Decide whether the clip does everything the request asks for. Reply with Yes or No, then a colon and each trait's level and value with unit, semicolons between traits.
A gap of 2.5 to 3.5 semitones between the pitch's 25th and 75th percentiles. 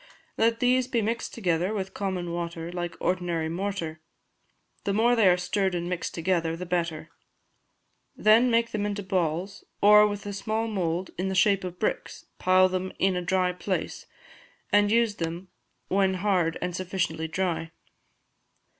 Yes: average, 2.8 semitones